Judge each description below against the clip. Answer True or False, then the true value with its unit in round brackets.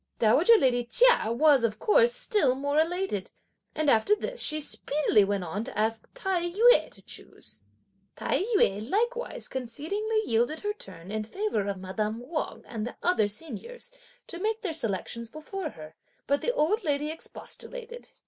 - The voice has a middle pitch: False (305 Hz)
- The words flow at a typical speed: True (160 wpm)